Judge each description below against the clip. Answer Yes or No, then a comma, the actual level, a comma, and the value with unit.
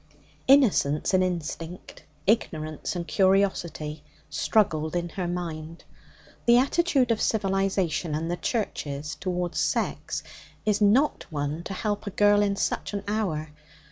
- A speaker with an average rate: No, slow, 130 wpm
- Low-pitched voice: No, medium, 185 Hz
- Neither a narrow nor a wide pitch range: Yes, average, 4.6 semitones